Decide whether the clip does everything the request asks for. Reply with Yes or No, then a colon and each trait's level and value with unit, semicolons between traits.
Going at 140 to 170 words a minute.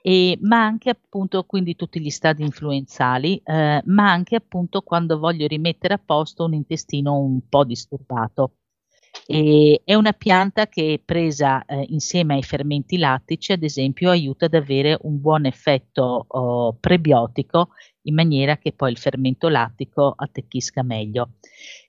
Yes: average, 145 wpm